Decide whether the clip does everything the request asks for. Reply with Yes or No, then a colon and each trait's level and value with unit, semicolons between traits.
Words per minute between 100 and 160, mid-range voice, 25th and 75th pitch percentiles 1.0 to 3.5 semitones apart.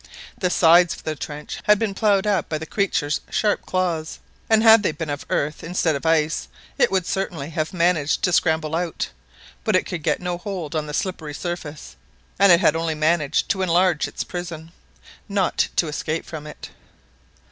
No: average, 190 wpm; medium, 165 Hz; average, 3.0 semitones